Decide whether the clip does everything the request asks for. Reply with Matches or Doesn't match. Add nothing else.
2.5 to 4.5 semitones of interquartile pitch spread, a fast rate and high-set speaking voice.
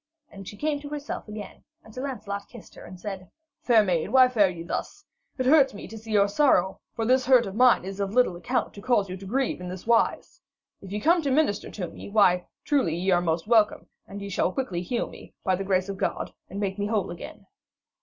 Doesn't match